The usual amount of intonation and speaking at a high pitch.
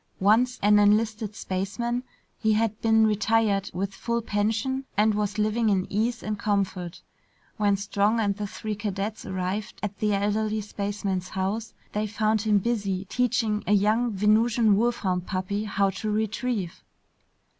No: narrow, 1.7 semitones; high, 210 Hz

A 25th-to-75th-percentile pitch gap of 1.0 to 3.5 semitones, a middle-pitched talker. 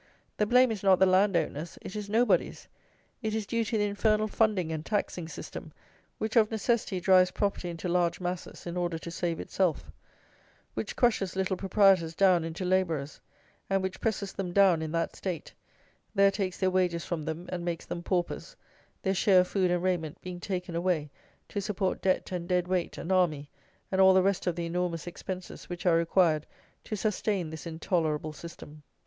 Yes: narrow, 2.6 semitones; medium, 180 Hz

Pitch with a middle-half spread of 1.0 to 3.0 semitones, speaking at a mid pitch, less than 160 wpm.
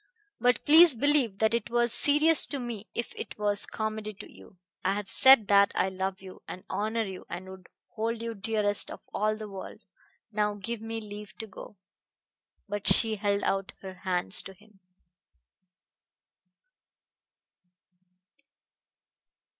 No: average, 2.7 semitones; high, 210 Hz; average, 145 wpm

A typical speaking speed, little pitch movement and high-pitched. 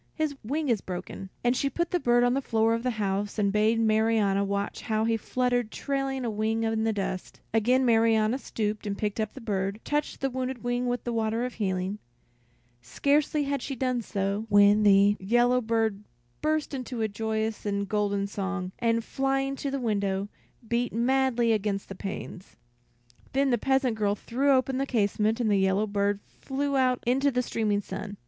No: average, 190 wpm; average, 3.8 semitones; high, 225 Hz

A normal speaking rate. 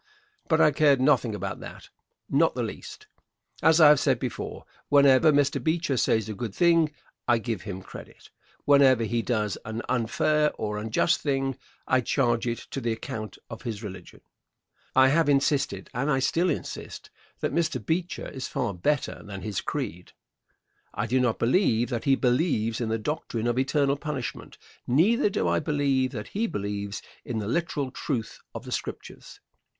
Yes: average, 170 wpm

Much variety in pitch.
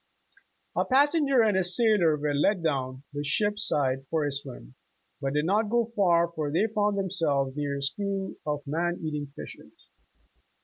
Yes: wide, 6.1 semitones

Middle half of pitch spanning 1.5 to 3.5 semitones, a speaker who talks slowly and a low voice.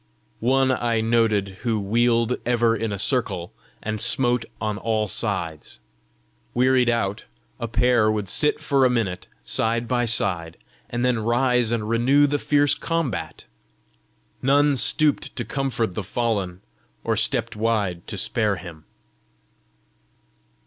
Yes: average, 3.0 semitones; slow, 130 wpm; low, 115 Hz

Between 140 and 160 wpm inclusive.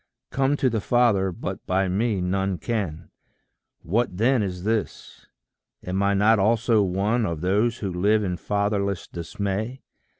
Yes: average, 145 wpm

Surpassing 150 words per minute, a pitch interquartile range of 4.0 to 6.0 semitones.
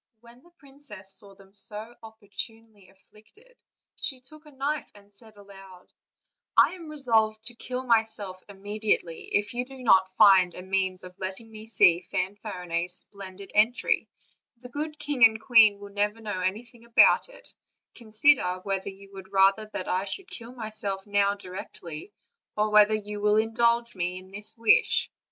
No: average, 160 wpm; average, 3.4 semitones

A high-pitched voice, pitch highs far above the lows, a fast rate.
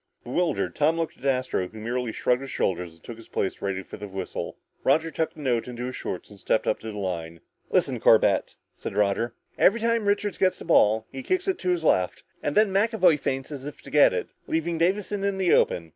No: low, 135 Hz; wide, 9.0 semitones; fast, 230 wpm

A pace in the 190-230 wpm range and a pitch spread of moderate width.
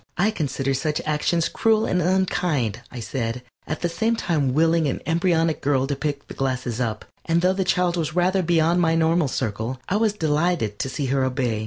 Yes: average, 200 wpm; average, 4.9 semitones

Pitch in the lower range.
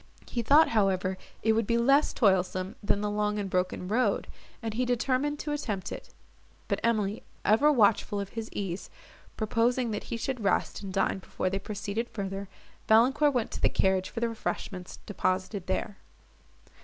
No: high, 210 Hz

